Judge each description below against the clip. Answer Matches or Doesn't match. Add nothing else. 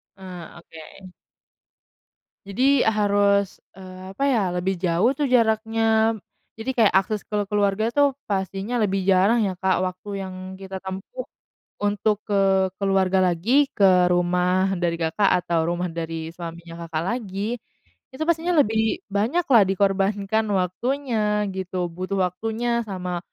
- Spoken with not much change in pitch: Doesn't match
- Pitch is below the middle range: Doesn't match